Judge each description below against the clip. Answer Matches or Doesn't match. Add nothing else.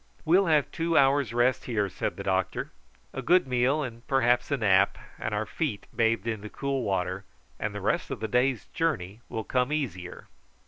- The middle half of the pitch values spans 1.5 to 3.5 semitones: Doesn't match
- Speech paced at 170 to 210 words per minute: Matches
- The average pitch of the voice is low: Matches